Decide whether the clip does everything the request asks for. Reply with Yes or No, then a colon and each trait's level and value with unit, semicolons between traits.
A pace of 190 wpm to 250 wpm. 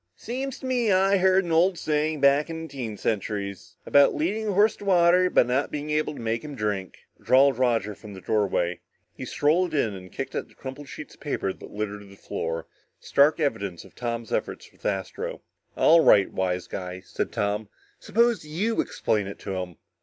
Yes: average, 200 wpm